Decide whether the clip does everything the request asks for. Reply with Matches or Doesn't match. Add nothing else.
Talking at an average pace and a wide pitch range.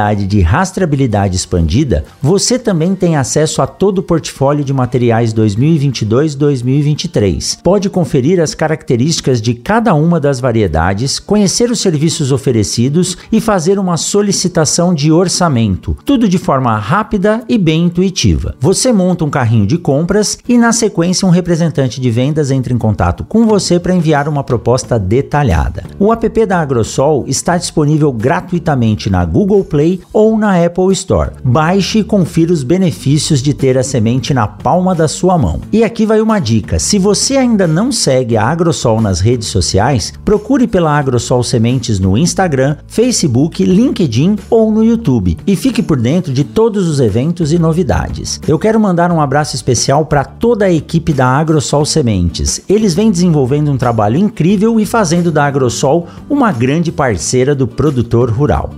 Matches